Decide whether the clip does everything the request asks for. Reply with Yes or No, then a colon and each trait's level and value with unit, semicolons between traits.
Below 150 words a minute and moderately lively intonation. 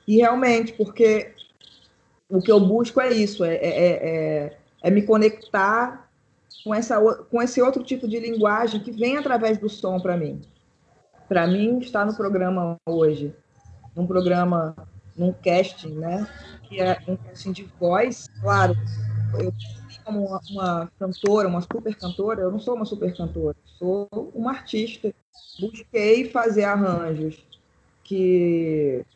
Yes: average, 140 wpm; average, 4.8 semitones